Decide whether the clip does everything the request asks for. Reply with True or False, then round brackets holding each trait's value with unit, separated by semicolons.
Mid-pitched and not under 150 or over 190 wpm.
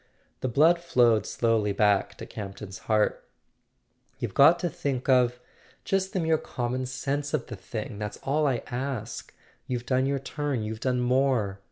False (125 Hz; 160 wpm)